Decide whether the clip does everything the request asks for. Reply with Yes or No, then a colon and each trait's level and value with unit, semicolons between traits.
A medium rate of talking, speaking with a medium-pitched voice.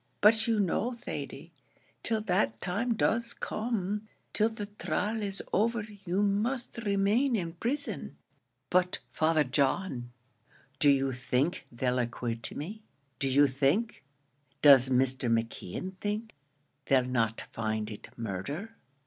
No: slow, 125 wpm; medium, 180 Hz